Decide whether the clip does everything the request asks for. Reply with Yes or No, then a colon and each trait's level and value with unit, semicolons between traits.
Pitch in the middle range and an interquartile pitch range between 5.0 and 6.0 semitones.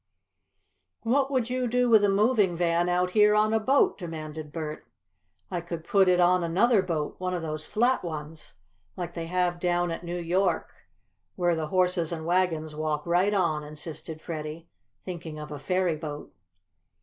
No: medium, 175 Hz; average, 3.3 semitones